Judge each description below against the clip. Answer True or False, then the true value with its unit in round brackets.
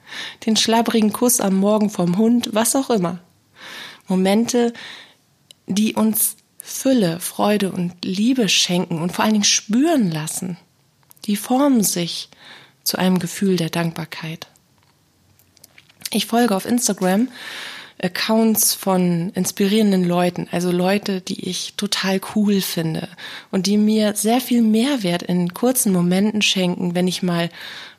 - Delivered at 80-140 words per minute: True (130 wpm)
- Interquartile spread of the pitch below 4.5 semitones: True (3.7 semitones)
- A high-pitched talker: True (195 Hz)